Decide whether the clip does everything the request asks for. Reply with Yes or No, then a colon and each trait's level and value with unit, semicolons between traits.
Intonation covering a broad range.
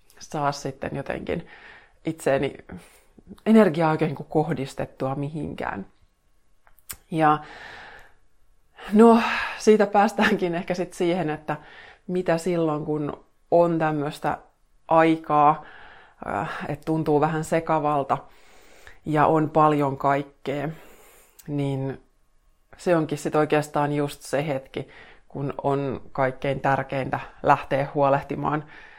No: average, 2.7 semitones